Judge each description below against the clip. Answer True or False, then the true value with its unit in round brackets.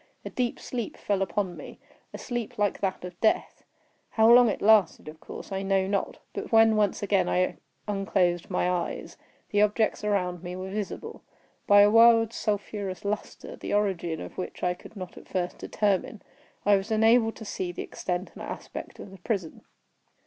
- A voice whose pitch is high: True (200 Hz)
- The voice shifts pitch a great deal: False (2.8 semitones)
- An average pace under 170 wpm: False (180 wpm)